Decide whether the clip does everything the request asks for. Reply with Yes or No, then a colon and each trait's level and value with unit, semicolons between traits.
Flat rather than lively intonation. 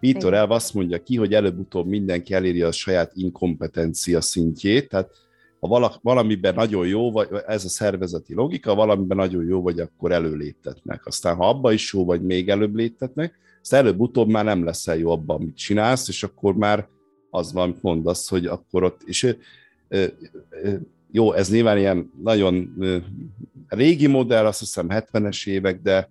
No: average, 3.4 semitones